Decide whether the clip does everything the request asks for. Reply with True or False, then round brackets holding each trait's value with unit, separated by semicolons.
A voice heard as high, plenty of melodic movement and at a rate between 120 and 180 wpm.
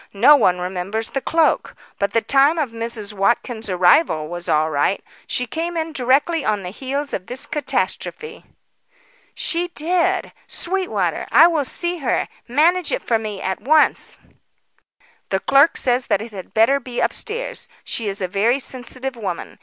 True (245 Hz; 7.3 semitones; 160 wpm)